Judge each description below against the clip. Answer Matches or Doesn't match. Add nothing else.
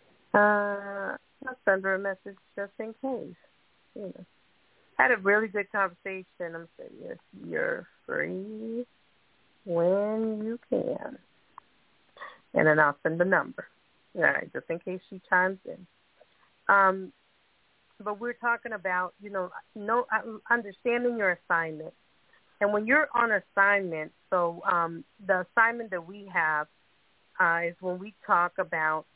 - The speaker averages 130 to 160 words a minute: Matches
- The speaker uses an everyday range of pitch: Matches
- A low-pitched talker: Doesn't match